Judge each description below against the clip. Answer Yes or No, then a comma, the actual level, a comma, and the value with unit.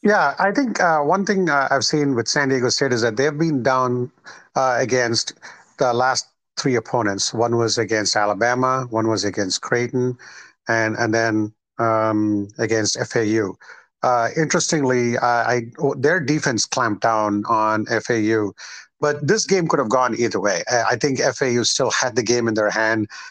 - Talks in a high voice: No, low, 120 Hz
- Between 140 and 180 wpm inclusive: Yes, average, 175 wpm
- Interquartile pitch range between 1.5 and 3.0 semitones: No, average, 3.6 semitones